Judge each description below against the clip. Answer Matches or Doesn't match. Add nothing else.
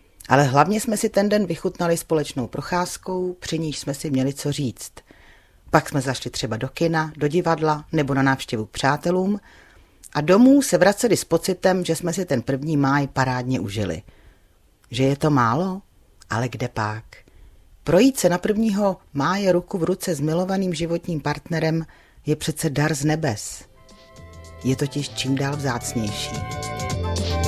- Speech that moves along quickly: Doesn't match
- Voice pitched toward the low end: Doesn't match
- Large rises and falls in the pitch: Matches